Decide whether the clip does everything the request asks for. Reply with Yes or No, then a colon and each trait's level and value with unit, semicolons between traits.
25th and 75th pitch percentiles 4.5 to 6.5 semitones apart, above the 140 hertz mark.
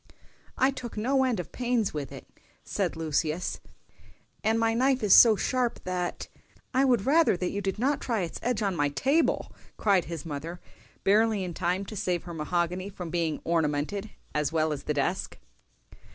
Yes: wide, 5.6 semitones; high, 190 Hz